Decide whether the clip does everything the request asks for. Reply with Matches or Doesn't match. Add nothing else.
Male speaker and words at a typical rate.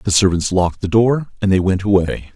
Doesn't match